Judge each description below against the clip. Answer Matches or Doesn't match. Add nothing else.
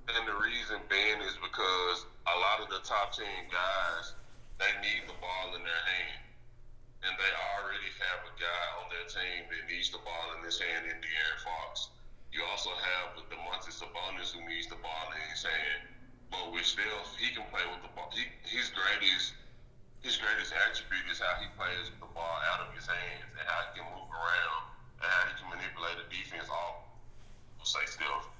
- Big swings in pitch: Matches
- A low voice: Matches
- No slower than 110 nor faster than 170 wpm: Doesn't match